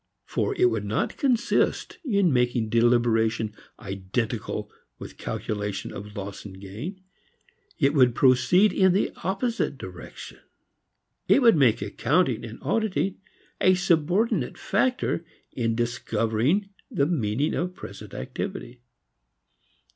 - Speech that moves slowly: Yes, slow, 115 wpm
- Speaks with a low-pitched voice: Yes, low, 125 Hz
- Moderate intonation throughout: No, wide, 8.9 semitones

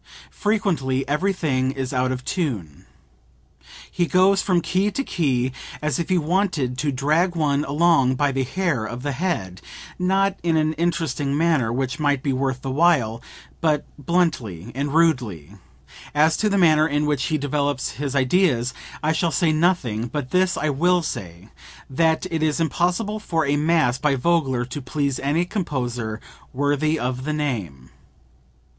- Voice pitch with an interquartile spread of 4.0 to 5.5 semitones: Yes, average, 4.7 semitones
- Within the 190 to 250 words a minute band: No, average, 160 wpm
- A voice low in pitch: No, medium, 145 Hz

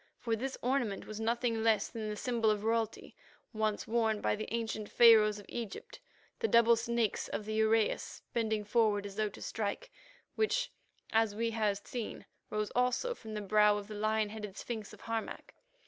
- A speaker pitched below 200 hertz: No, high, 220 Hz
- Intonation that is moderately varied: No, narrow, 1.7 semitones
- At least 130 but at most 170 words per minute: No, average, 180 wpm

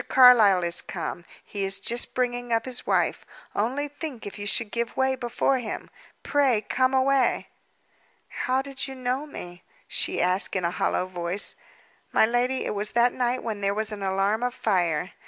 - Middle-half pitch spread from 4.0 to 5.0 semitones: Yes, average, 4.5 semitones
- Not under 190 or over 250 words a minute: No, average, 180 wpm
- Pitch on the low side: No, high, 235 Hz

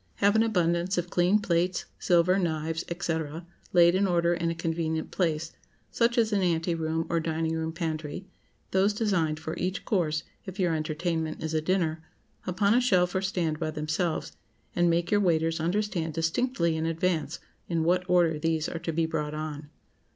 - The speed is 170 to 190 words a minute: Yes, average, 175 wpm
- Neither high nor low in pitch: Yes, medium, 170 Hz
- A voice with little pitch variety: Yes, narrow, 2.3 semitones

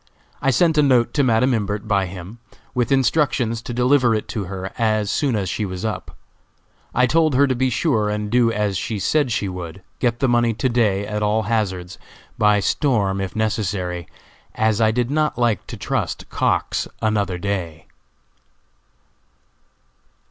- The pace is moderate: Yes, average, 170 wpm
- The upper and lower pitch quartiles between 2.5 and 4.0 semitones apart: Yes, average, 3.7 semitones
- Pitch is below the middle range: Yes, low, 110 Hz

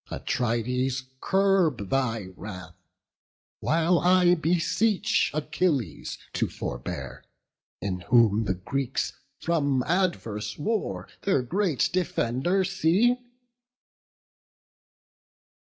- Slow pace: Yes, slow, 80 wpm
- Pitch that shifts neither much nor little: No, wide, 7.8 semitones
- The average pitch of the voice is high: No, medium, 145 Hz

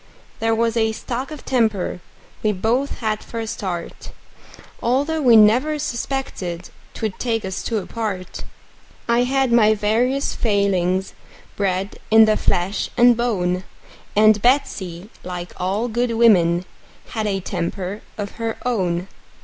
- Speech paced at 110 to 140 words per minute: Yes, slow, 135 wpm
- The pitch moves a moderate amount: Yes, average, 4.0 semitones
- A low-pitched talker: No, high, 220 Hz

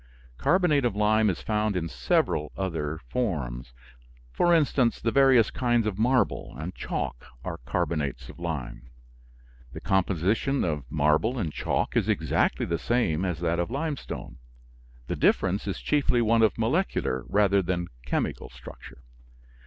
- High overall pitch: No, very low, 95 Hz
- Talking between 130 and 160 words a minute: Yes, average, 145 wpm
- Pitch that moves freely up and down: Yes, wide, 7.5 semitones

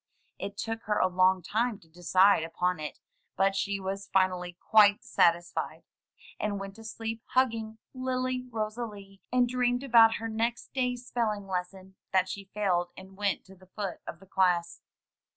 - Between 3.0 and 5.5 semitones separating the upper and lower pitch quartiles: Yes, average, 3.4 semitones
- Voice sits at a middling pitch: No, high, 200 Hz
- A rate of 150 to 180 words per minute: Yes, average, 170 wpm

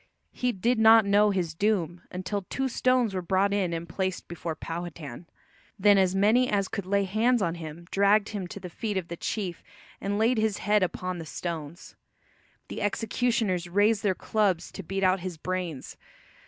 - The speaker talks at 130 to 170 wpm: No, average, 180 wpm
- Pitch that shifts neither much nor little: Yes, average, 3.3 semitones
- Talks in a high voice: Yes, high, 195 Hz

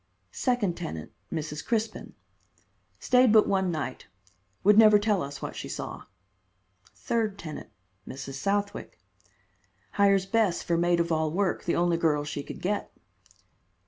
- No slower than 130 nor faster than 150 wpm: Yes, average, 140 wpm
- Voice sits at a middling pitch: Yes, medium, 180 Hz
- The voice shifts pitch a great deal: No, average, 4.7 semitones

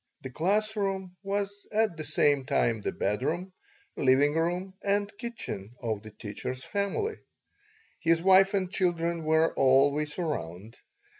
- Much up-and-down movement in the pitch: Yes, wide, 6.6 semitones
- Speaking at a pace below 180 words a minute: Yes, slow, 135 wpm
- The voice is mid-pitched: Yes, medium, 165 Hz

